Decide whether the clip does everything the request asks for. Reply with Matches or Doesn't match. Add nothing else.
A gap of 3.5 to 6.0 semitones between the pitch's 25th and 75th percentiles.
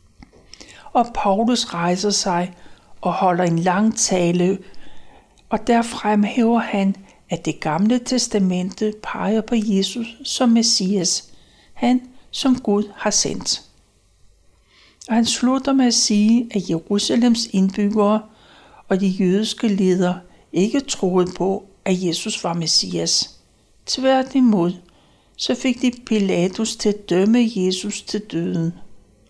Matches